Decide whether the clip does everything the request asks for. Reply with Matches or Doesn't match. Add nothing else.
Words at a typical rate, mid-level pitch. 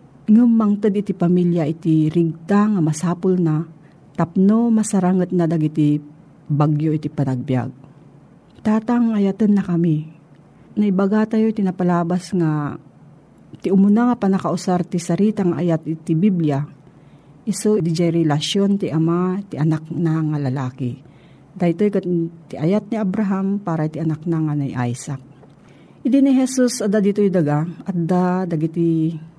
Matches